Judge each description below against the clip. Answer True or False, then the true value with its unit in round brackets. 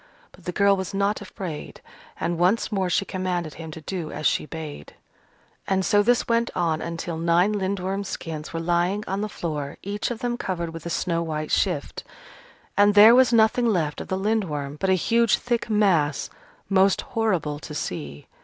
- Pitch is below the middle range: False (185 Hz)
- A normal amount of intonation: True (4.0 semitones)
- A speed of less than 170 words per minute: False (185 wpm)